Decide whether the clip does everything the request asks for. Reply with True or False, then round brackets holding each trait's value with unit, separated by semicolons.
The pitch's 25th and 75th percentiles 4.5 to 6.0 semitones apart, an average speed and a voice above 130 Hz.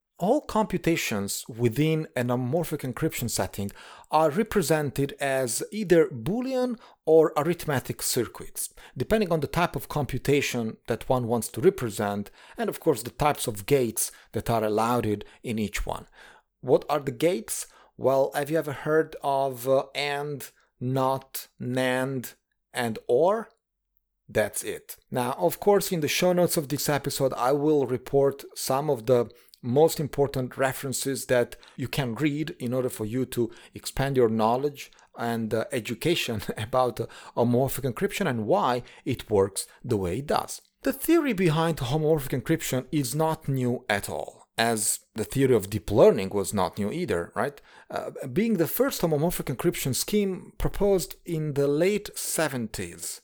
True (5.0 semitones; 155 wpm; 140 Hz)